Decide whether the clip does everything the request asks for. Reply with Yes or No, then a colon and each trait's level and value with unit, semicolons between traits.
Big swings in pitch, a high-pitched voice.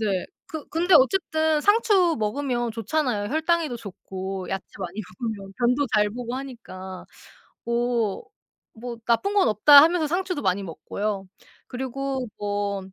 Yes: wide, 6.9 semitones; high, 240 Hz